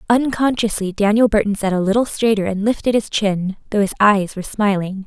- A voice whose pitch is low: No, high, 210 Hz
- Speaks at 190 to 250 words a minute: No, average, 180 wpm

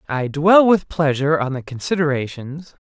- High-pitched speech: No, medium, 150 Hz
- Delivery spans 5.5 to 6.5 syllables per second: No, 5.0 syllables/s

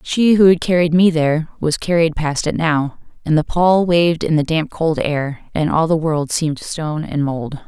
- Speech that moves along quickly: Yes, fast, 220 wpm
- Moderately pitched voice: Yes, medium, 160 Hz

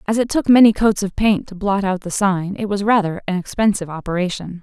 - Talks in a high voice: Yes, high, 195 Hz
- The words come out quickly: Yes, fast, 235 wpm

